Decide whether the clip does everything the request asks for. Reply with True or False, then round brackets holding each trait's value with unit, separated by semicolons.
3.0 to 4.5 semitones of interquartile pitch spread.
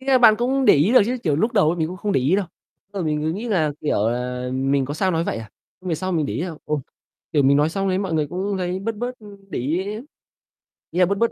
False (5.2 semitones)